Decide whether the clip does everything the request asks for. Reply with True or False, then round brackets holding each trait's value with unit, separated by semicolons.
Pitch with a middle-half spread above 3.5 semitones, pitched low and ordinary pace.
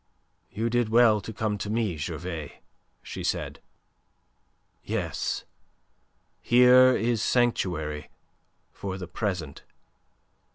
False (5.2 semitones; 105 Hz; 95 wpm)